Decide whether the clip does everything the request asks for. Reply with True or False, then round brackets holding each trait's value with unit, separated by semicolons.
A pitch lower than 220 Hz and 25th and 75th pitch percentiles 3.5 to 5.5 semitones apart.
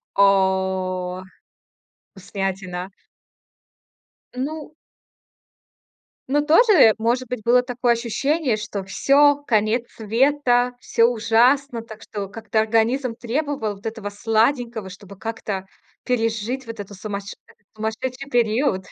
False (225 Hz; 3.8 semitones)